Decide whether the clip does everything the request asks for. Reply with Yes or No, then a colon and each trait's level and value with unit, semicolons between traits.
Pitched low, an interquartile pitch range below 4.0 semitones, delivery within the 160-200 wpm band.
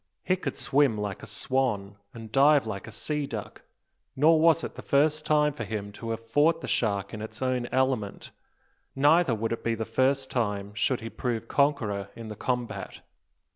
No: low, 120 Hz; average, 4.6 semitones; average, 190 wpm